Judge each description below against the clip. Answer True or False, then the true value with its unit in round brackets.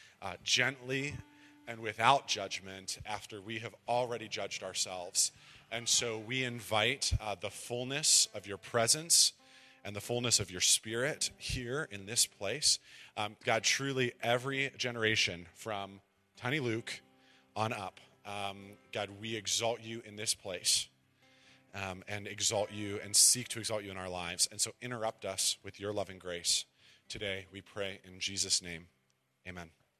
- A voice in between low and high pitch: False (105 Hz)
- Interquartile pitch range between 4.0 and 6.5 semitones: False (3.4 semitones)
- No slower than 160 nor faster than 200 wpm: False (150 wpm)